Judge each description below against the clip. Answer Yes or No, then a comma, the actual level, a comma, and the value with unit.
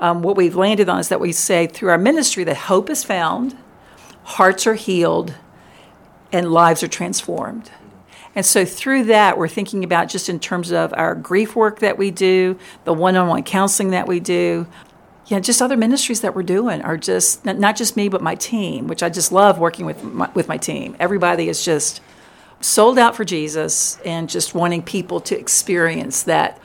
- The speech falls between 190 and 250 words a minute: Yes, average, 195 wpm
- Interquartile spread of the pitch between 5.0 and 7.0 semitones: No, average, 3.5 semitones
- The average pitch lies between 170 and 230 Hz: Yes, medium, 185 Hz